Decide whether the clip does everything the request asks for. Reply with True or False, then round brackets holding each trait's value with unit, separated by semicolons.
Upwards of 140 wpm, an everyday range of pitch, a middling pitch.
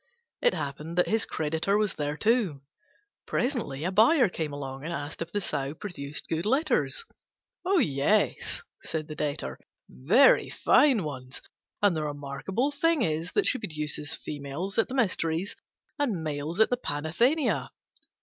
False (150 wpm; 7.2 semitones; 165 Hz)